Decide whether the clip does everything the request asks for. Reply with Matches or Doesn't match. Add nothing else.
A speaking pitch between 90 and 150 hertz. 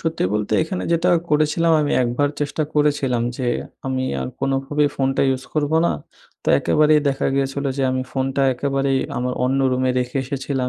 Matches